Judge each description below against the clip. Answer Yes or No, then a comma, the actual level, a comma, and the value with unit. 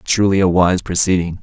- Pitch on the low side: Yes, very low, 90 Hz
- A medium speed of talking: Yes, average, 170 wpm